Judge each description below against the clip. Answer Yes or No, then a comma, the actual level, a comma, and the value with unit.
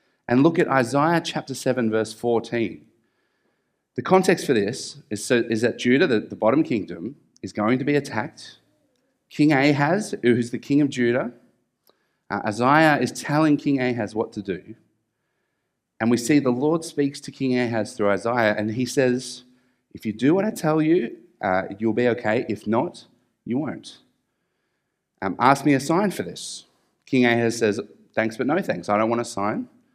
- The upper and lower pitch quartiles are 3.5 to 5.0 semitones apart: Yes, average, 4.4 semitones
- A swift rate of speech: No, average, 180 wpm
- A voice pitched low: Yes, low, 125 Hz